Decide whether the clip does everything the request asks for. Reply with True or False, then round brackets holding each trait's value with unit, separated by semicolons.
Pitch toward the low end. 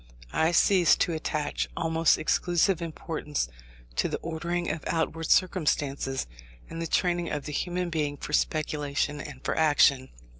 False (160 Hz)